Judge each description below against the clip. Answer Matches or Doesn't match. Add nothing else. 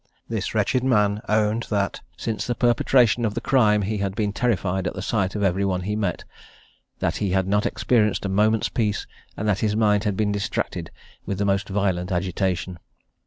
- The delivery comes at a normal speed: Matches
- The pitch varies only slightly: Matches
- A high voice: Doesn't match